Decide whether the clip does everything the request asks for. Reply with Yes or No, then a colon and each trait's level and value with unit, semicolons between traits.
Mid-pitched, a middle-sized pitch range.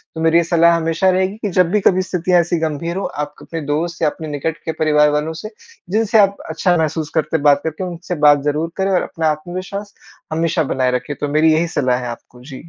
Yes: medium, 165 Hz; average, 3.2 semitones